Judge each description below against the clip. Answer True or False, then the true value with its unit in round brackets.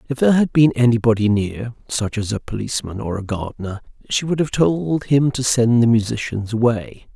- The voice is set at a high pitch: False (120 Hz)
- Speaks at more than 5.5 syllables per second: False (5.4 syllables/s)